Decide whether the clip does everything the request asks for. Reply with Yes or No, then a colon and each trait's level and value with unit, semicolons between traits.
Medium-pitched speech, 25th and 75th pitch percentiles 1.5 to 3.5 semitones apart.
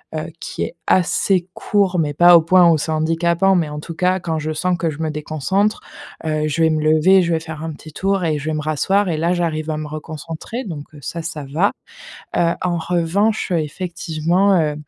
Yes: medium, 165 Hz; average, 2.7 semitones